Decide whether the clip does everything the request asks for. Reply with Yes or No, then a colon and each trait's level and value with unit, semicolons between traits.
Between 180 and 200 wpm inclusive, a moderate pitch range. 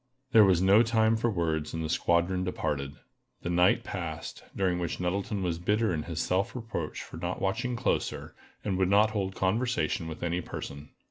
Yes: average, 185 wpm; average, 3.9 semitones